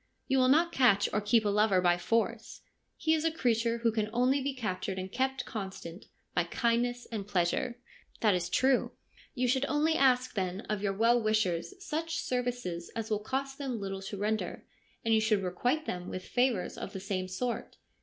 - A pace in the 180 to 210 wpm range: Yes, average, 200 wpm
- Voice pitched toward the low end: No, high, 225 Hz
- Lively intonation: No, average, 4.5 semitones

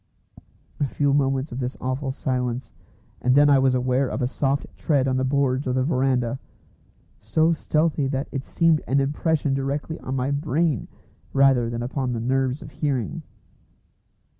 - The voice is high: No, low, 135 Hz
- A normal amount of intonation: No, narrow, 2.0 semitones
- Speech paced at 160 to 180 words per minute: Yes, average, 165 wpm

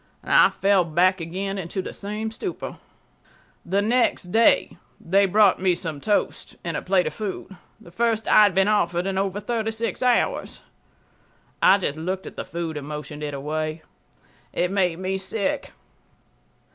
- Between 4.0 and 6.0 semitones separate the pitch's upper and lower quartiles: No, average, 3.4 semitones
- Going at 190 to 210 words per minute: No, average, 160 wpm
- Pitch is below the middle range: No, high, 190 Hz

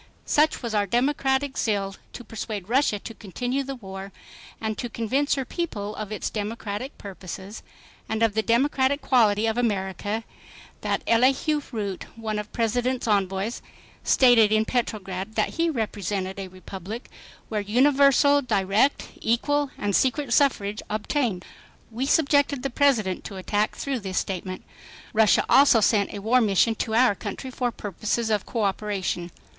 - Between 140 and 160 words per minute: Yes, average, 150 wpm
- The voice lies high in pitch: Yes, high, 220 Hz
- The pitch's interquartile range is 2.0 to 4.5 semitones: Yes, average, 4.1 semitones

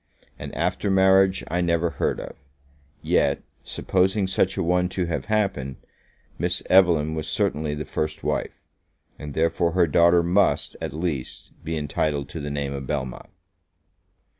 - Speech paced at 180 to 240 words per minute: No, average, 150 wpm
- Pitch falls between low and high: No, very low, 85 Hz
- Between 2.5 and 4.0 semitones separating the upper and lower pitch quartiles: Yes, average, 3.7 semitones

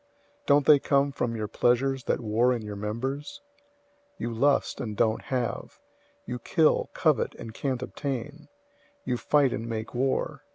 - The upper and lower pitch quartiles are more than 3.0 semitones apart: Yes, average, 3.4 semitones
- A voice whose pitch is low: Yes, low, 125 Hz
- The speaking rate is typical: Yes, average, 160 wpm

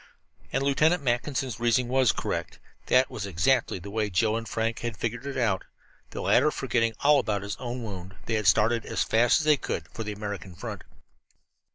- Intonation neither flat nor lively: Yes, average, 3.8 semitones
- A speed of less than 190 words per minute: No, average, 200 wpm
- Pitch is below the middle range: Yes, low, 115 Hz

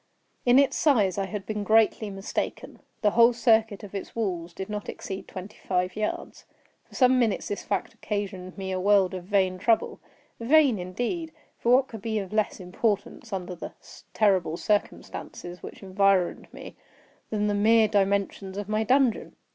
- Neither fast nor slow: Yes, average, 170 wpm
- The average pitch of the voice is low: No, high, 205 Hz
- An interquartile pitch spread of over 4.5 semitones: No, average, 2.7 semitones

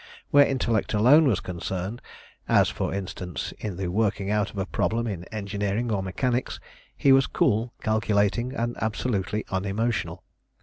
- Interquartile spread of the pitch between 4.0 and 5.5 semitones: No, average, 3.3 semitones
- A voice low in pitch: Yes, low, 105 Hz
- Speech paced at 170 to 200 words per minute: No, average, 145 wpm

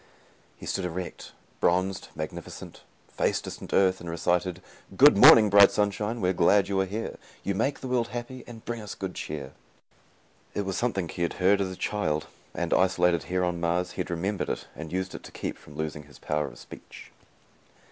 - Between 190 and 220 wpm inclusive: Yes, average, 195 wpm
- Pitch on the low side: Yes, very low, 95 Hz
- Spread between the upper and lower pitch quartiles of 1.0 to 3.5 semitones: Yes, average, 3.0 semitones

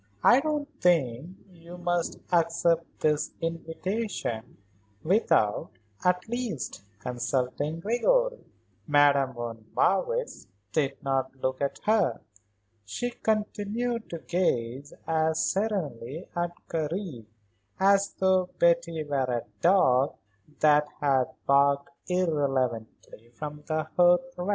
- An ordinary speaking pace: No, slow, 110 wpm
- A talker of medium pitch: Yes, medium, 165 Hz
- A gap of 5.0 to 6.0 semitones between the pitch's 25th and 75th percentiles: Yes, wide, 5.6 semitones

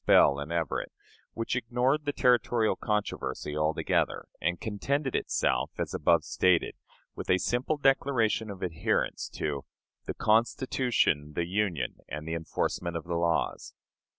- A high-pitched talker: No, low, 100 Hz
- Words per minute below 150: Yes, slow, 135 wpm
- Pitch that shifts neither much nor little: No, wide, 6.8 semitones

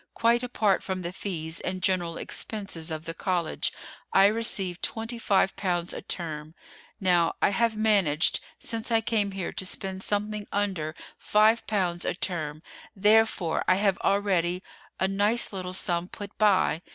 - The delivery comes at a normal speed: Yes, average, 155 wpm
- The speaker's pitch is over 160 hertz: Yes, high, 190 Hz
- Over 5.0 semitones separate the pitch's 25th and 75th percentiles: No, average, 3.3 semitones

